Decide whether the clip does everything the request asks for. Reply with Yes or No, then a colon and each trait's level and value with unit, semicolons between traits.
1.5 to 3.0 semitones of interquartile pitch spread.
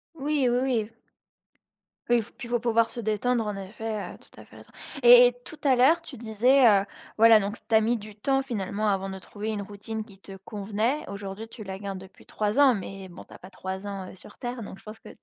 No: average, 3.4 semitones